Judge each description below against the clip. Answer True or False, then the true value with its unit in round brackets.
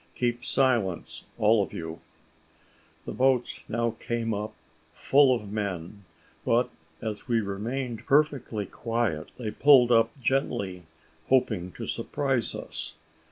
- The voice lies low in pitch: True (115 Hz)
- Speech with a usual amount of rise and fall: True (3.7 semitones)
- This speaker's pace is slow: True (120 wpm)